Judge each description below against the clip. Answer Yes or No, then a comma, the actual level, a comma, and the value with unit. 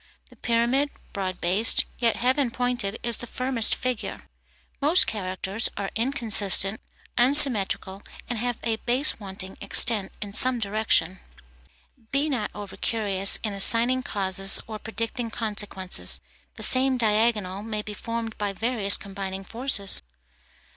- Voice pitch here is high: Yes, high, 220 Hz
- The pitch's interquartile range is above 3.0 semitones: Yes, average, 3.5 semitones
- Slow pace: Yes, slow, 130 wpm